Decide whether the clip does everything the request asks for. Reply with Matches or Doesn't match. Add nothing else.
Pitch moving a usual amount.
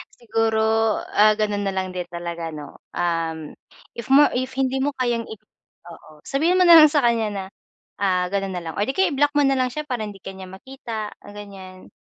Doesn't match